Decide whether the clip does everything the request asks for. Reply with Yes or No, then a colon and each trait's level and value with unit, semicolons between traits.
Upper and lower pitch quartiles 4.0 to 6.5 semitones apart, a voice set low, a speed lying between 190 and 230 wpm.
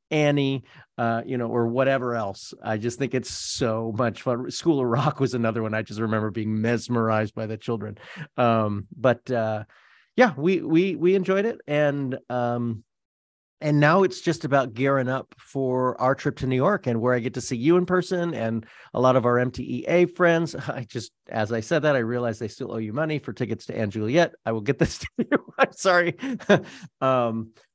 Yes: average, 4.7 semitones; low, 125 Hz; fast, 205 wpm